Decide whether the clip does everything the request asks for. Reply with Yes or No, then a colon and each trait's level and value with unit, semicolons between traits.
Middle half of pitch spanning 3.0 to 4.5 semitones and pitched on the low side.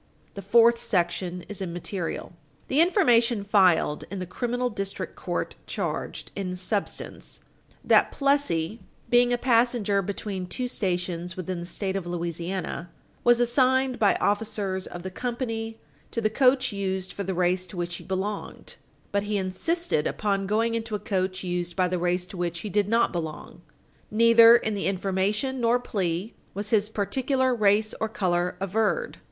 No: average, 4.2 semitones; high, 200 Hz